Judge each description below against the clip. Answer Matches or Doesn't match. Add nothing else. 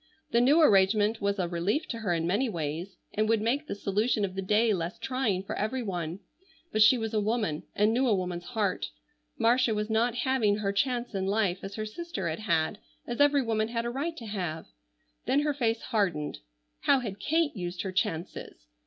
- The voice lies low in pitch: Doesn't match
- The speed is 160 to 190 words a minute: Doesn't match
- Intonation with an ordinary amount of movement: Matches